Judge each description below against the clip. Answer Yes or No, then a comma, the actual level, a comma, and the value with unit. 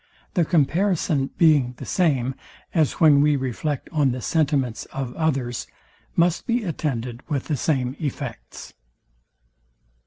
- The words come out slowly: Yes, slow, 125 wpm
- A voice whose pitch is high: No, medium, 145 Hz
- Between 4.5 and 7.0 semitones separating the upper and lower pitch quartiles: No, average, 3.8 semitones